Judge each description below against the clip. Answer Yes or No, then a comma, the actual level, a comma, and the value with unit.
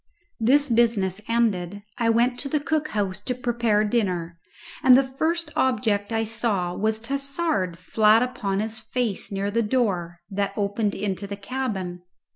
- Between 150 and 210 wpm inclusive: Yes, average, 155 wpm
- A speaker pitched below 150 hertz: No, high, 220 Hz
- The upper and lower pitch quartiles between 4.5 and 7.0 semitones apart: No, average, 3.9 semitones